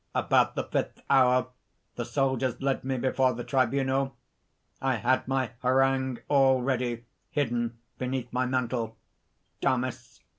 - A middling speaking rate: No, slow, 125 wpm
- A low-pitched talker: Yes, low, 130 Hz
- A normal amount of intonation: No, narrow, 1.6 semitones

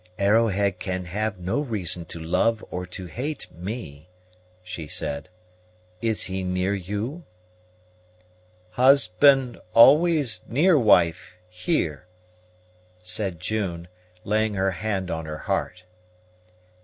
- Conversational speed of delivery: No, slow, 105 wpm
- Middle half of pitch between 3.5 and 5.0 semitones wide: Yes, average, 4.3 semitones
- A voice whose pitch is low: Yes, very low, 95 Hz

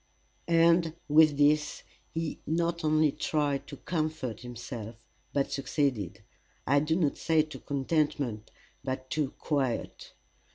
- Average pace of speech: No, slow, 120 wpm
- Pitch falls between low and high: Yes, medium, 150 Hz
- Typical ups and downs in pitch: Yes, average, 3.1 semitones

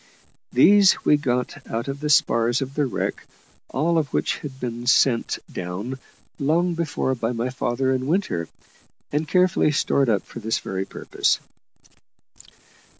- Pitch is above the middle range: No, low, 130 Hz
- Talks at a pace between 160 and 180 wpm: No, average, 150 wpm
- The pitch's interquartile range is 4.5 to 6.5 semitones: No, average, 4.1 semitones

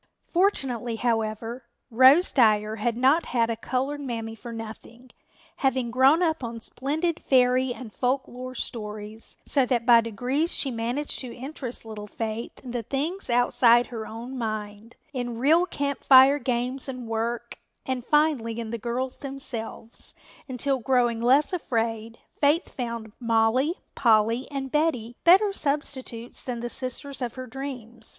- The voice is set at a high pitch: Yes, high, 245 Hz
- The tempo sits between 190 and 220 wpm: No, average, 150 wpm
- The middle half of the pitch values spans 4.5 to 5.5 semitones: No, average, 2.9 semitones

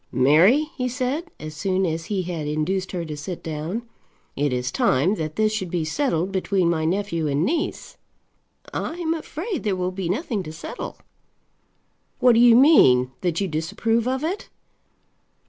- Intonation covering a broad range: Yes, wide, 7.4 semitones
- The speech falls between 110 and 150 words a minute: No, average, 170 wpm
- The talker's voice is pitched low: No, medium, 185 Hz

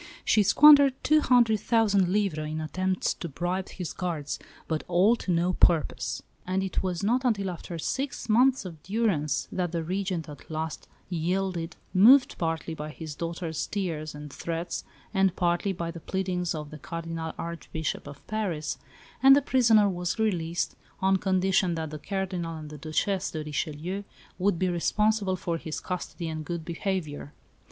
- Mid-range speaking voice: Yes, medium, 180 Hz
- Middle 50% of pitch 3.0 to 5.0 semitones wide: Yes, average, 3.4 semitones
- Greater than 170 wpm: No, average, 165 wpm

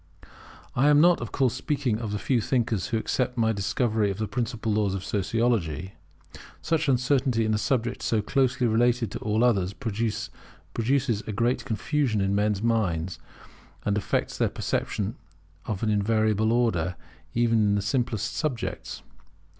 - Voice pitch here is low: Yes, low, 110 Hz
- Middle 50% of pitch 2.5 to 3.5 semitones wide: Yes, average, 3.0 semitones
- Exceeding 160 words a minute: No, average, 155 wpm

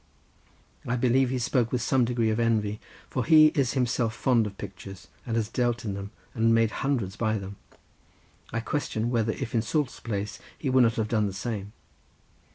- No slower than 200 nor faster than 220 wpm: No, average, 190 wpm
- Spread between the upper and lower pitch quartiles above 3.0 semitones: No, average, 2.7 semitones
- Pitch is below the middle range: Yes, low, 115 Hz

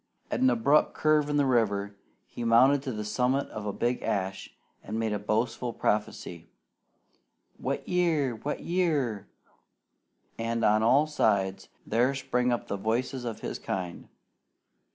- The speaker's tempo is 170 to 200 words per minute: No, average, 145 wpm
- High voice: No, low, 120 Hz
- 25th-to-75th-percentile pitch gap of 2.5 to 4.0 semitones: No, average, 4.8 semitones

